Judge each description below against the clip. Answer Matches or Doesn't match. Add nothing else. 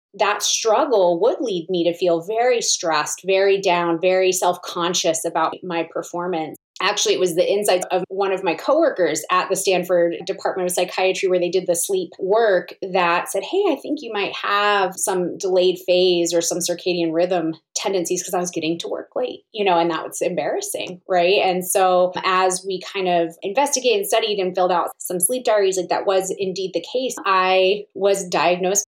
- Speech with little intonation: Matches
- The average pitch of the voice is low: Doesn't match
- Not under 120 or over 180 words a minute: Doesn't match